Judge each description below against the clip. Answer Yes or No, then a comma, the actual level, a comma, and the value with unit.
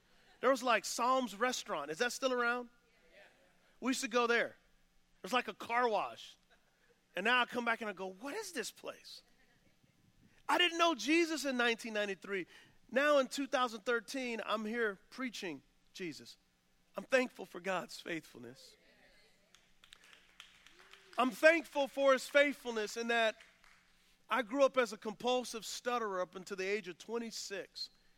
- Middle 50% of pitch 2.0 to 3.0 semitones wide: No, average, 3.8 semitones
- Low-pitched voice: No, high, 240 Hz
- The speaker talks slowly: No, average, 150 wpm